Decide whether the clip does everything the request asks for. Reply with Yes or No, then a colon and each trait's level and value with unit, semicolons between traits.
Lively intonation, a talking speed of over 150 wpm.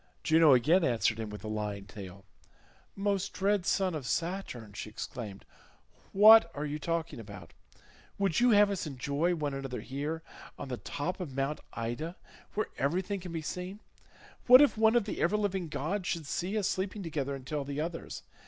Yes: wide, 6.5 semitones; average, 180 wpm